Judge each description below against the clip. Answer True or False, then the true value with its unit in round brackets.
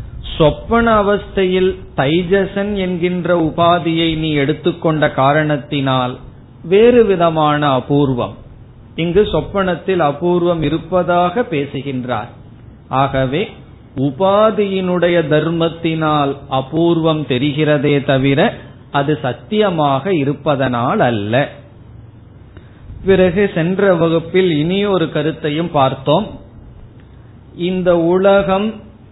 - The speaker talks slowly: True (70 wpm)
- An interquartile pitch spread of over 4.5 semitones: True (5.2 semitones)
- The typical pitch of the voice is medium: True (150 Hz)